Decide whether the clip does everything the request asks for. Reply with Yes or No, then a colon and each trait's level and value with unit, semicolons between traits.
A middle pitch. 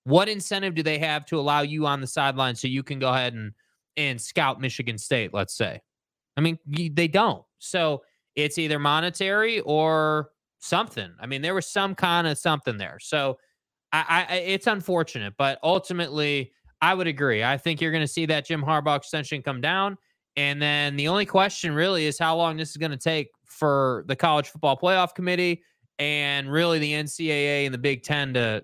Yes: medium, 150 Hz